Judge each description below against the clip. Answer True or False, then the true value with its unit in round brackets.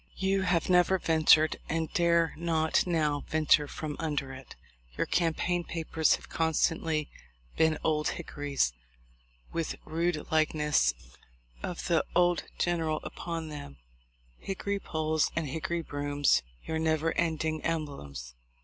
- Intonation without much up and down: True (1.9 semitones)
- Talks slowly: True (125 wpm)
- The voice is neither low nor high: True (160 Hz)